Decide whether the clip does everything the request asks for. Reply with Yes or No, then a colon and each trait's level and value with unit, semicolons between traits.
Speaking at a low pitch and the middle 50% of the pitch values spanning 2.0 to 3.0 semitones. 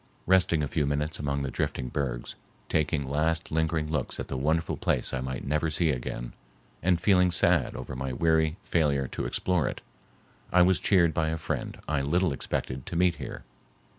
No: very low, 80 Hz; average, 3.5 semitones